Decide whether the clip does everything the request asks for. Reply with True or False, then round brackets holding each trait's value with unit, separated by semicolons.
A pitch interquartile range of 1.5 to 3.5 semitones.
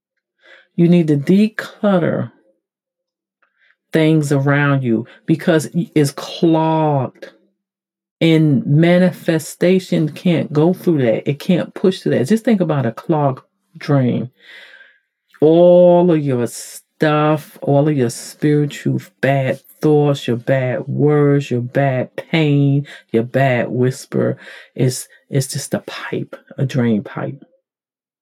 False (4.4 semitones)